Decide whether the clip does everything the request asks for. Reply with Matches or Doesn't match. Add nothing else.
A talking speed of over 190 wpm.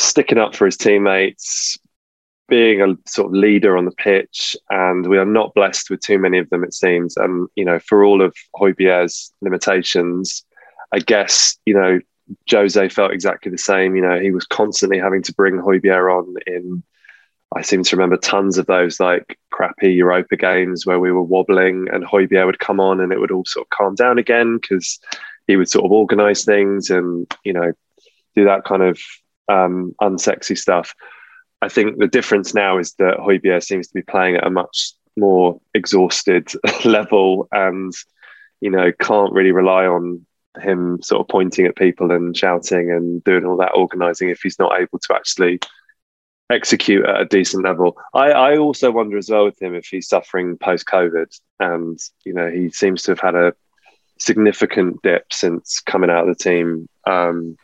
Doesn't match